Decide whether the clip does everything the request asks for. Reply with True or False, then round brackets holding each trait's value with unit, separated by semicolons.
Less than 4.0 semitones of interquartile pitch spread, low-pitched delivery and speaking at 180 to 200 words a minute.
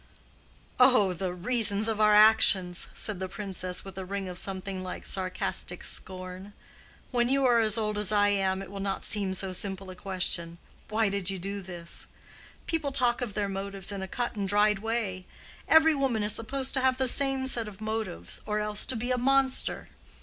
False (3.5 semitones; 205 Hz; 190 wpm)